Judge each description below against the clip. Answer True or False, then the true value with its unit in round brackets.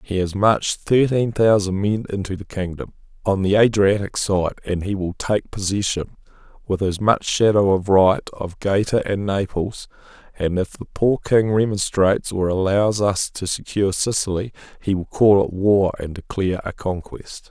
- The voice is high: False (100 Hz)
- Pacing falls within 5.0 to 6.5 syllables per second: False (4.7 syllables/s)